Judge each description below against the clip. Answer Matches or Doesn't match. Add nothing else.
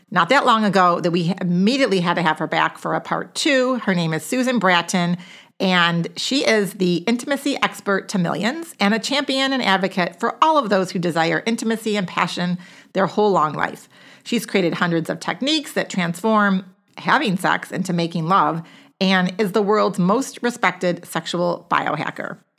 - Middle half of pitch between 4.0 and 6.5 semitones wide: Matches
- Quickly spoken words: Doesn't match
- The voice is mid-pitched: Doesn't match